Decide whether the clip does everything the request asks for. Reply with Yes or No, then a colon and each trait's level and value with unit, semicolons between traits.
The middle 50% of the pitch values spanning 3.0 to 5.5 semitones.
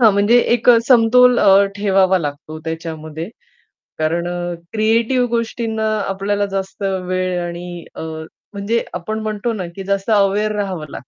Yes: average, 3.8 semitones